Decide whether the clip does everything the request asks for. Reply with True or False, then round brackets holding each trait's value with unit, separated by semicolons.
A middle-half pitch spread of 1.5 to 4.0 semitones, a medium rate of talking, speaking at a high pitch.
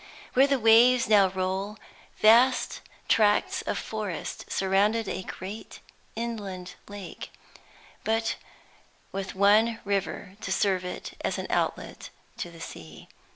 False (2.9 semitones; 120 wpm; 205 Hz)